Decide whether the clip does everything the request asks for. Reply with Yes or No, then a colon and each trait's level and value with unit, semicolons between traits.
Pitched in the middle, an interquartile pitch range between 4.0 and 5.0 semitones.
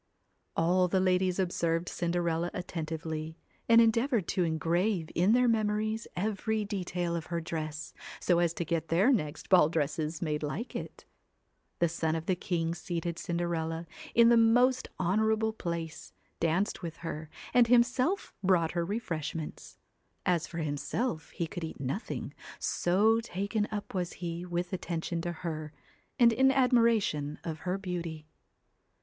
Yes: medium, 175 Hz; average, 4.5 semitones